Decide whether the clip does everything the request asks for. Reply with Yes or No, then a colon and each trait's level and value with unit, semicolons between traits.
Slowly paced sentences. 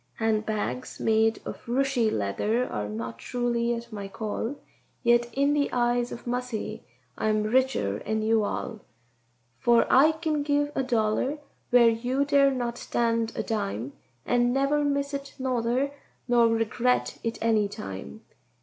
No: average, 150 wpm